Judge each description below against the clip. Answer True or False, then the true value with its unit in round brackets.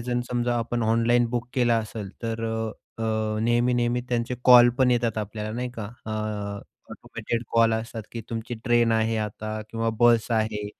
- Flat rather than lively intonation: True (1.5 semitones)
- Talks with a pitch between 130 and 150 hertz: False (115 Hz)